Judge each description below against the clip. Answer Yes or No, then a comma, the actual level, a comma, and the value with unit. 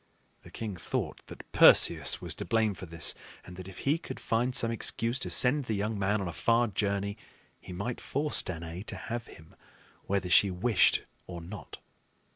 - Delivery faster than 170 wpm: Yes, average, 190 wpm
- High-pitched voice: No, low, 100 Hz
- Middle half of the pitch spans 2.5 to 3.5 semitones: No, average, 4.2 semitones